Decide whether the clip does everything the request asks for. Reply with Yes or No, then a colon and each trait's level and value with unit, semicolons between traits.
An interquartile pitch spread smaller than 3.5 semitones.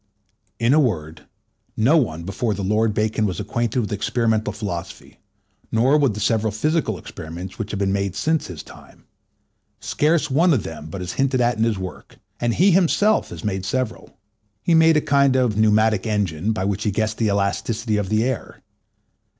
No: average, 4.4 semitones